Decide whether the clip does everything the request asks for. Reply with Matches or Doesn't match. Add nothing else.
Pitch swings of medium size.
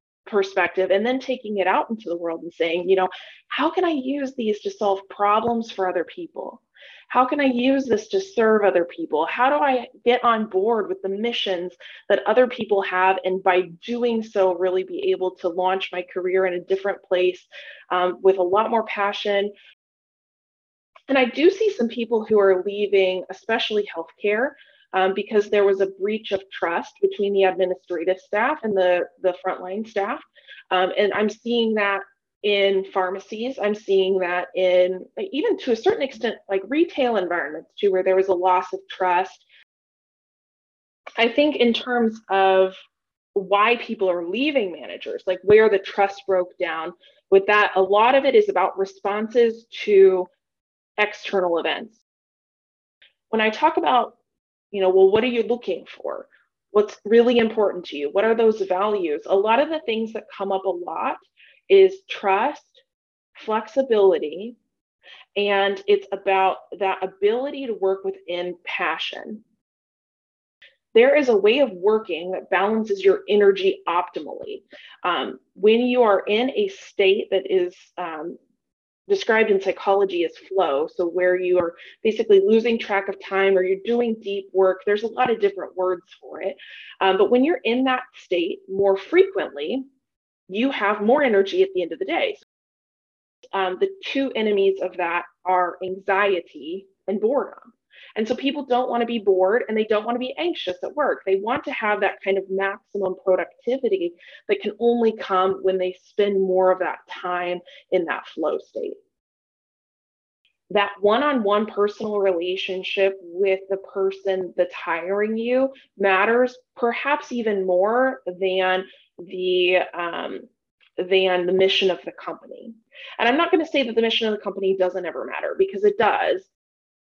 Matches